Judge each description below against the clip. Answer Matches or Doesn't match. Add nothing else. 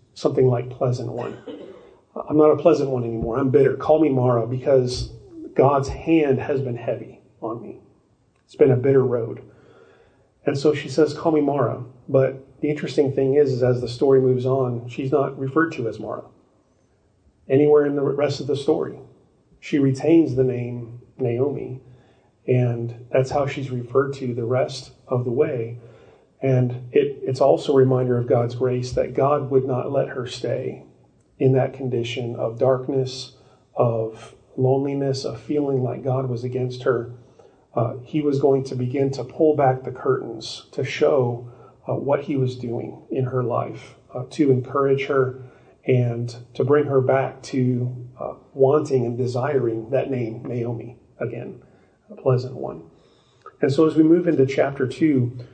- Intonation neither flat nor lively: Doesn't match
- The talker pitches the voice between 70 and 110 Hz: Doesn't match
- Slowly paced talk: Doesn't match